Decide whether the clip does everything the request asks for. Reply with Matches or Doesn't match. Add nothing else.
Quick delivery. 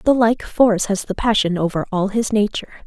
Matches